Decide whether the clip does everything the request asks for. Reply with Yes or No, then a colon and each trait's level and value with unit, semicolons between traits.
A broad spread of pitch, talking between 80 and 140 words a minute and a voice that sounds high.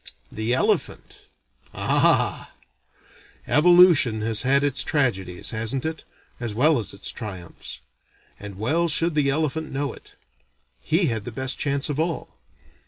No: wide, 5.7 semitones; slow, 135 wpm; low, 135 Hz